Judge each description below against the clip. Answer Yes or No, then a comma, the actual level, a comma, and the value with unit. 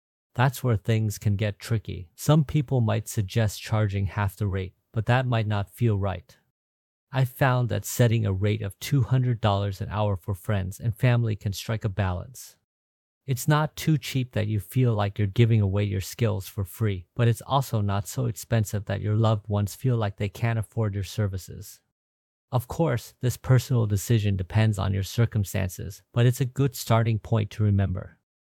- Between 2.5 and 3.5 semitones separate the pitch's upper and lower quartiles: Yes, average, 3.2 semitones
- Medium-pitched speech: No, low, 110 Hz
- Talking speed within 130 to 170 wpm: No, average, 185 wpm